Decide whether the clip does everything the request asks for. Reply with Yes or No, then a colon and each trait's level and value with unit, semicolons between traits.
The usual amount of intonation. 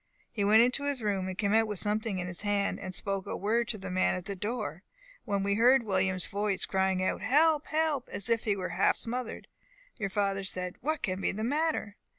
Yes: average, 3.6 semitones